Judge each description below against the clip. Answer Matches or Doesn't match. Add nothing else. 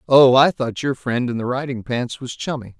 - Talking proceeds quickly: Matches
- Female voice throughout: Doesn't match